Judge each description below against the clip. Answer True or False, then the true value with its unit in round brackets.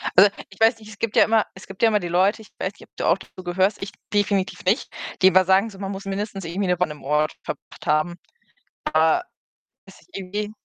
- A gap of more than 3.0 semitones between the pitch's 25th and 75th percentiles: False (2.5 semitones)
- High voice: True (195 Hz)